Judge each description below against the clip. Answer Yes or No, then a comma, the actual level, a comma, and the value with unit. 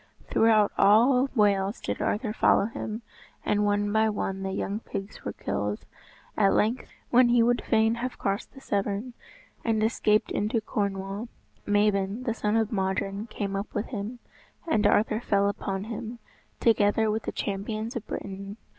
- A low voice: No, high, 210 Hz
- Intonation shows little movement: Yes, narrow, 2.2 semitones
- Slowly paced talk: No, average, 160 wpm